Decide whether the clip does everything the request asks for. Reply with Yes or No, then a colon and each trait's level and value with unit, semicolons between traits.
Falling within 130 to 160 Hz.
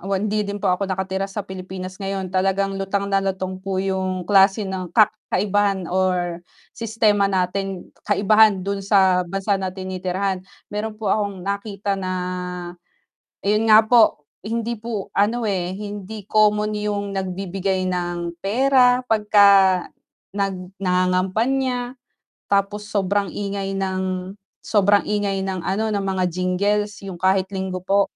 No: high, 195 Hz